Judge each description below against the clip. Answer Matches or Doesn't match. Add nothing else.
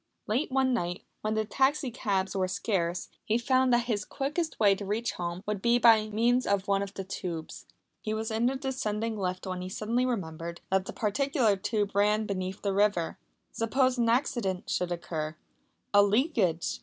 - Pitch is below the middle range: Doesn't match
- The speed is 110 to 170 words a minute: Doesn't match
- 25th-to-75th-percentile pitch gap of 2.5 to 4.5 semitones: Matches